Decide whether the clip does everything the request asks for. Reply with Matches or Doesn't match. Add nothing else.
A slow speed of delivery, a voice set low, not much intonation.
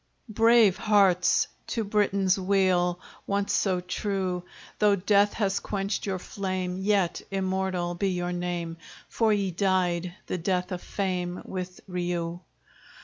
Doesn't match